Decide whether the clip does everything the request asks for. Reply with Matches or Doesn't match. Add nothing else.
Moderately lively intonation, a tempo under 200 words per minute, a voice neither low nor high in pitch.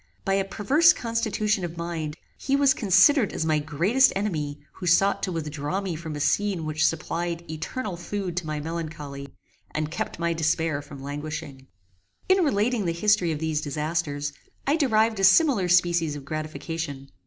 Matches